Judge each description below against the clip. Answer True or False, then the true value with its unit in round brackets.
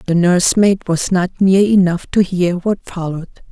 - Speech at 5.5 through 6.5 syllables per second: False (4.9 syllables/s)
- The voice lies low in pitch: False (185 Hz)